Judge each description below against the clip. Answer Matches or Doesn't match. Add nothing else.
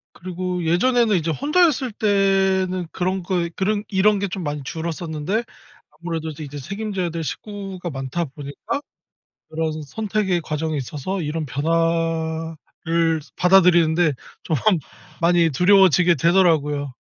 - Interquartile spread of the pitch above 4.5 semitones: Doesn't match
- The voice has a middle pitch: Matches